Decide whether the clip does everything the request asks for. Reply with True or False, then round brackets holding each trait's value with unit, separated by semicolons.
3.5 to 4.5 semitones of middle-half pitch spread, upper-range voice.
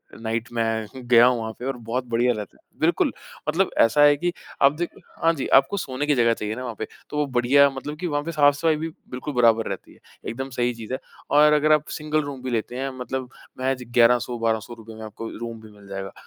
False (3.9 semitones; 125 Hz)